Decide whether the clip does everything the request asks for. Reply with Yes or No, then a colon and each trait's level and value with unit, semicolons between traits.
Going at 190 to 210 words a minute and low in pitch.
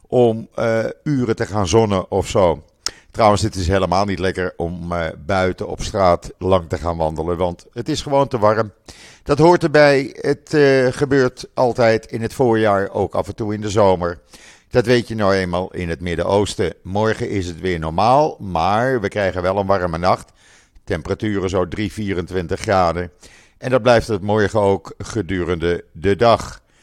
No: average, 175 wpm; low, 100 Hz